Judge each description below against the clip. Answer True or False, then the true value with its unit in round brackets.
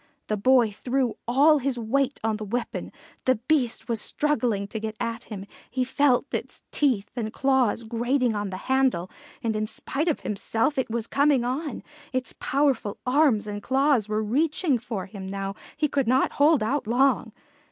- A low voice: False (245 Hz)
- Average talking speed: True (175 wpm)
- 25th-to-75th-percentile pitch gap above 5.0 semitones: False (4.0 semitones)